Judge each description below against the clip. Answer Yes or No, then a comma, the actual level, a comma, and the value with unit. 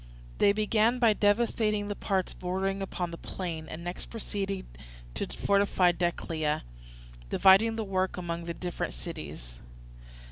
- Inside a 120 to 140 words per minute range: Yes, slow, 135 wpm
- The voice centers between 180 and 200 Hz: Yes, high, 190 Hz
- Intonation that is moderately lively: Yes, average, 3.1 semitones